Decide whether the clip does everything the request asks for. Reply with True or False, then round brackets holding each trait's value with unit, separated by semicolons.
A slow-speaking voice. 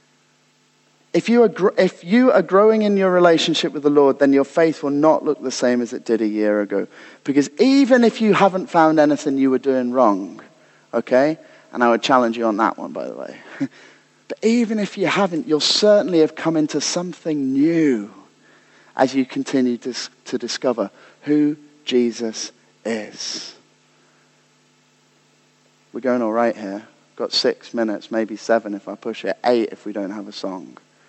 False (180 wpm)